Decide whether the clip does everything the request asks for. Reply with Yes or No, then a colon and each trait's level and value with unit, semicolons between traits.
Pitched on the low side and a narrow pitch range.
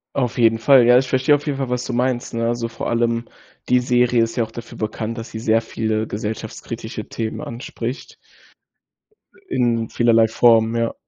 Yes: low, 115 Hz; narrow, 1.5 semitones